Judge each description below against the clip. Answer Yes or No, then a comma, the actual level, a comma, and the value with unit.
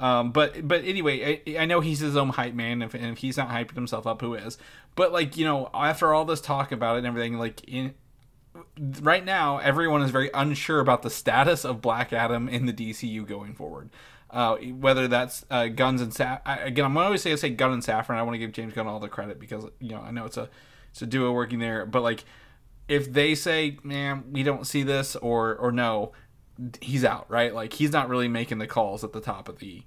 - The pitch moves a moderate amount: Yes, average, 3.7 semitones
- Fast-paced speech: Yes, fast, 245 wpm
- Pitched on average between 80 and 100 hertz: No, low, 125 Hz